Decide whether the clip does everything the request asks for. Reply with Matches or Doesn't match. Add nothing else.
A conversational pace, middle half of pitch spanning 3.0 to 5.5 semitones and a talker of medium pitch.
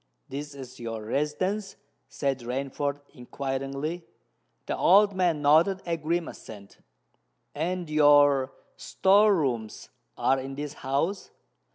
Doesn't match